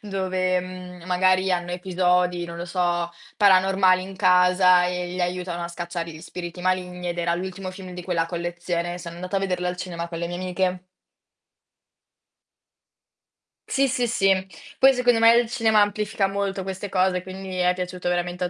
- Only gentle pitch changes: Yes, narrow, 1.3 semitones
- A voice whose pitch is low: No, medium, 180 Hz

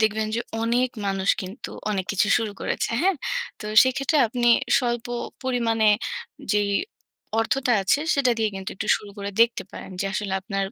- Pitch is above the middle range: Yes, high, 225 Hz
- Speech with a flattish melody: No, average, 3.4 semitones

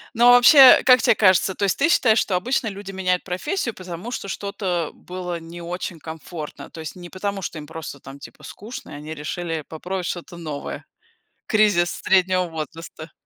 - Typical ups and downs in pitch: Yes, average, 3.7 semitones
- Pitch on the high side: No, medium, 180 Hz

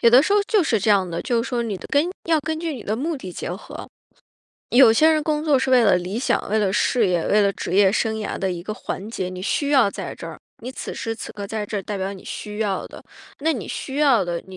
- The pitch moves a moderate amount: No, wide, 5.7 semitones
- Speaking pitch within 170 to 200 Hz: No, high, 220 Hz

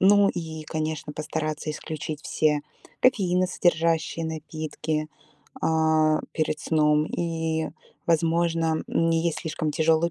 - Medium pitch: Yes, medium, 160 Hz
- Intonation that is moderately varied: No, narrow, 1.4 semitones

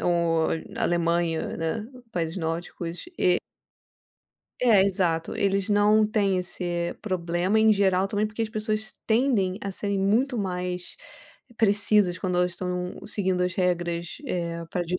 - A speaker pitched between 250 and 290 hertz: No, medium, 185 Hz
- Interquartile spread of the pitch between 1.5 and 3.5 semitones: Yes, average, 3.0 semitones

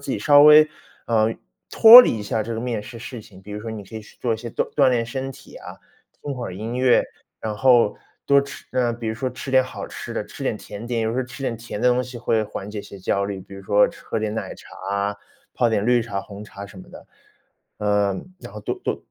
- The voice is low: Yes, low, 115 Hz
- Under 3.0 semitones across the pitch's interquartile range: No, average, 3.3 semitones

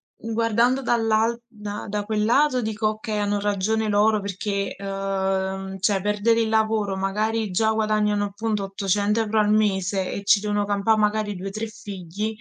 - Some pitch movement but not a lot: No, narrow, 1.8 semitones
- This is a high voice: Yes, high, 210 Hz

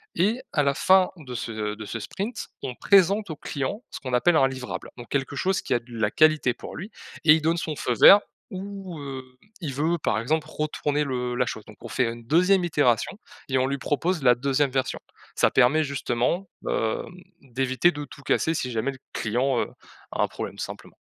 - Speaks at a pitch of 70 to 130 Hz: No, medium, 140 Hz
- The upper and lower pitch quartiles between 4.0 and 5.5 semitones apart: Yes, average, 5.0 semitones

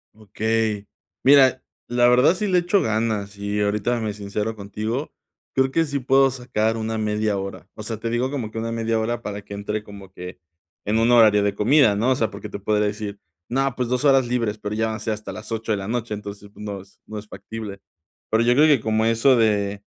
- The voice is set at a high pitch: No, low, 110 Hz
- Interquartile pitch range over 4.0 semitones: No, average, 2.8 semitones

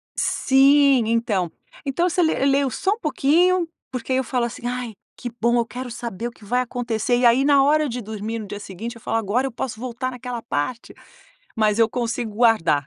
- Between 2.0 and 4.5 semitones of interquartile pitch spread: Yes, average, 2.9 semitones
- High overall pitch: Yes, high, 240 Hz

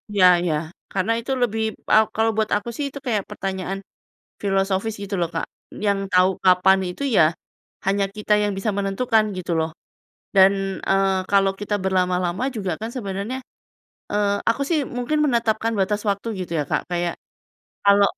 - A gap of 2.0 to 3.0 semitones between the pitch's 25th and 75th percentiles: Yes, average, 2.7 semitones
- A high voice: Yes, high, 200 Hz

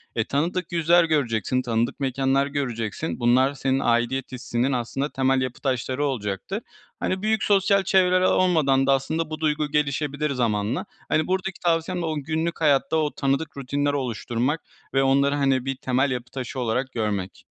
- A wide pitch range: No, average, 3.8 semitones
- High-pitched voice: No, medium, 140 Hz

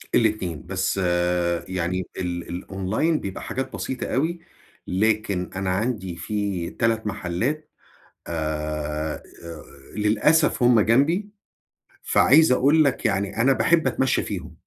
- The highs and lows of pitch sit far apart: Yes, wide, 6.5 semitones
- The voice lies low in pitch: Yes, low, 105 Hz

